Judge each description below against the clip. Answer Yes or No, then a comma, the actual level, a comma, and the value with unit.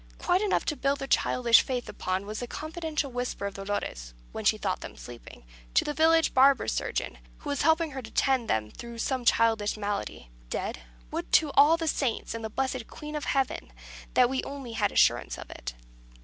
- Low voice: No, very high, 255 Hz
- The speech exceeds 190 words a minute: Yes, average, 200 wpm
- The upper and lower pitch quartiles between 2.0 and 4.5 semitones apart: No, average, 5.1 semitones